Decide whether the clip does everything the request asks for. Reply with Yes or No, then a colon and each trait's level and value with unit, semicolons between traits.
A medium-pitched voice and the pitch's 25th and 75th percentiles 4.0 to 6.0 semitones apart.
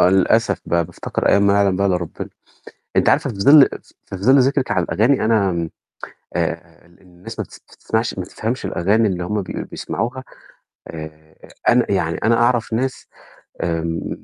No: low, 100 Hz; average, 4.8 semitones